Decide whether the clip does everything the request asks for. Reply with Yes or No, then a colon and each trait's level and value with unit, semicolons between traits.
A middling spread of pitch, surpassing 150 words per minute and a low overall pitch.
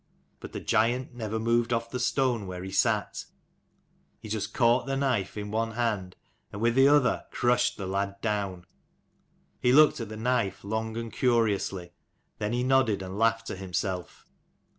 Yes: average, 3.4 semitones; average, 170 wpm; low, 115 Hz